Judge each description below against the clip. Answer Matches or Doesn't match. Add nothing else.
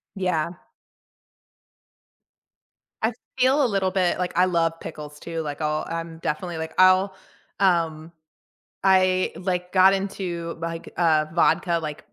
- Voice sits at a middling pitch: Matches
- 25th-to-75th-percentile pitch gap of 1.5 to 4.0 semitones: Matches